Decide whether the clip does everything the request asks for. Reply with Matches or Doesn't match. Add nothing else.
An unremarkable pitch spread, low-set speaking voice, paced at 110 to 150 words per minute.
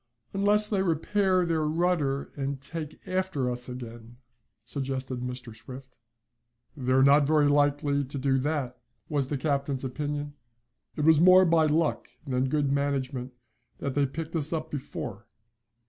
Doesn't match